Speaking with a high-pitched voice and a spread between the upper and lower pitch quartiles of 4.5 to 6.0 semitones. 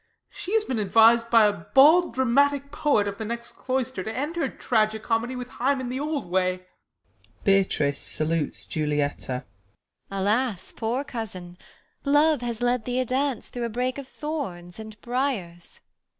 Yes: high, 235 Hz; average, 5.1 semitones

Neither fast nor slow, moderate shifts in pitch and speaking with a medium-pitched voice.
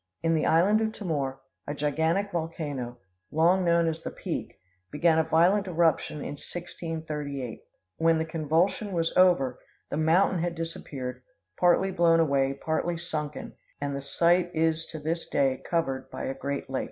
Yes: average, 160 wpm; average, 3.0 semitones; medium, 160 Hz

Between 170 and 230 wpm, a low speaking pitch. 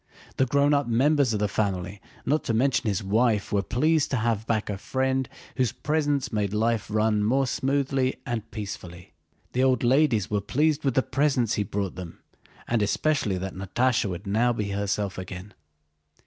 Yes: average, 175 wpm; low, 115 Hz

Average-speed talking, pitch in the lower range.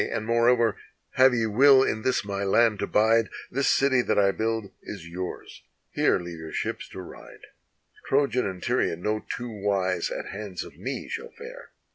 Yes: average, 180 wpm; low, 110 Hz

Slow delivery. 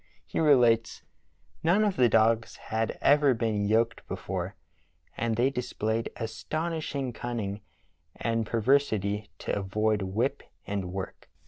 Yes: slow, 120 wpm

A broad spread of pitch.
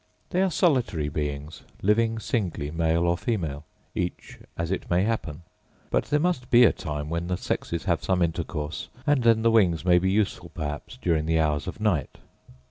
Yes: wide, 6.1 semitones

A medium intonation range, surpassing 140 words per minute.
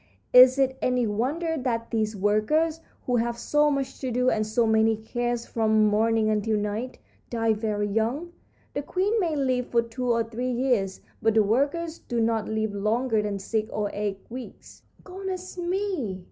Yes: average, 3.7 semitones; average, 175 wpm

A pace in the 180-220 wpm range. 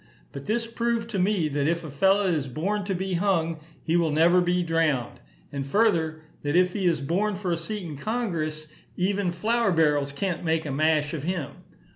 Yes: average, 200 wpm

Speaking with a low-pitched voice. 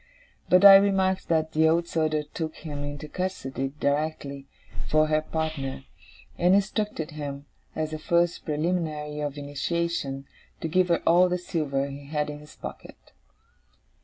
No: medium, 155 Hz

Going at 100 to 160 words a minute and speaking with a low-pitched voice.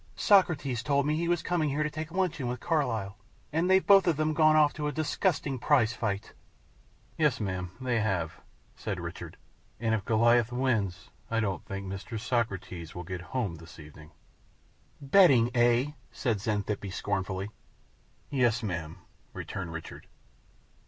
Yes: average, 150 wpm; low, 120 Hz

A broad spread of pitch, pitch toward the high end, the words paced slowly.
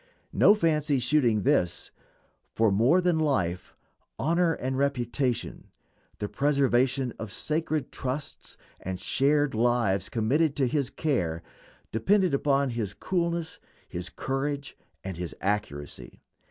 No: wide, 5.8 semitones; low, 135 Hz; slow, 115 wpm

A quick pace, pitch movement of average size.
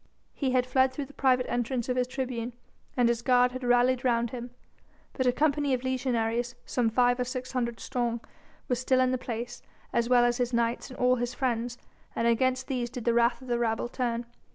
No: fast, 215 wpm; narrow, 1.3 semitones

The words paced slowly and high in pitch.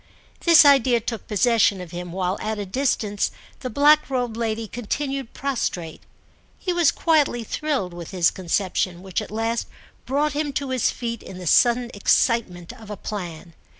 No: average, 165 wpm; high, 230 Hz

